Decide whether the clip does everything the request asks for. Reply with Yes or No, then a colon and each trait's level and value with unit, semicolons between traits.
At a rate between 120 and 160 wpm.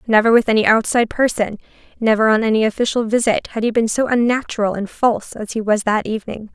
No: average, 200 wpm